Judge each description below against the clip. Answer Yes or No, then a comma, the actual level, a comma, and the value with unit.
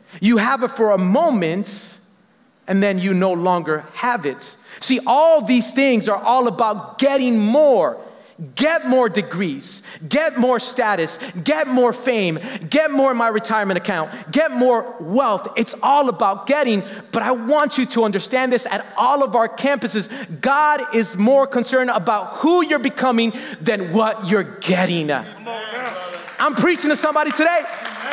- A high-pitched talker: Yes, high, 235 Hz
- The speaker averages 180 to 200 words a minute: No, average, 155 wpm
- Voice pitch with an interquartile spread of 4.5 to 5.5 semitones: Yes, average, 5.1 semitones